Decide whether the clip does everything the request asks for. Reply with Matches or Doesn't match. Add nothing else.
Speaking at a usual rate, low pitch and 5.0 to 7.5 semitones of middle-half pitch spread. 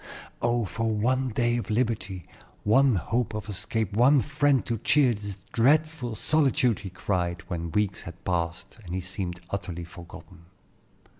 Matches